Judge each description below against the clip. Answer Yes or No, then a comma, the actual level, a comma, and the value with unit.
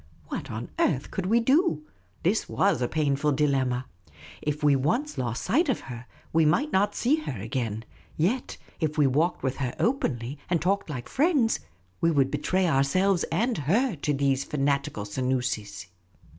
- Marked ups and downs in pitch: Yes, wide, 7.0 semitones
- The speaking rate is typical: Yes, average, 165 wpm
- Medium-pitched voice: Yes, medium, 150 Hz